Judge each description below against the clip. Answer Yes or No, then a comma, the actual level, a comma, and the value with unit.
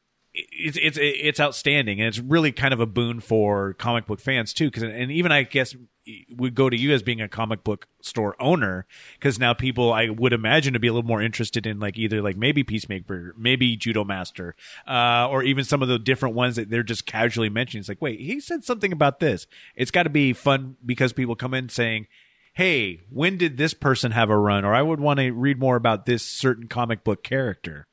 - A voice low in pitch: Yes, low, 120 Hz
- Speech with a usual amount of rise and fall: Yes, average, 3.6 semitones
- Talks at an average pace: No, fast, 225 wpm